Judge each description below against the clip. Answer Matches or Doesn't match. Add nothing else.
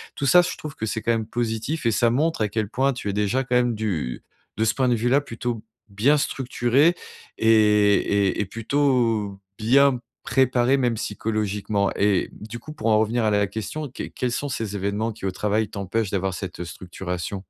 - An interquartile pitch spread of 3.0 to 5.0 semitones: Matches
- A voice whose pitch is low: Matches